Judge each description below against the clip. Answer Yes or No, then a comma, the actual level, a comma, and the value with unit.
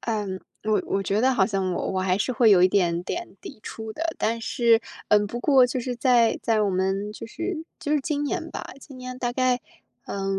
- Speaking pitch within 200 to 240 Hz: Yes, high, 225 Hz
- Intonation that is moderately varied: Yes, average, 4.4 semitones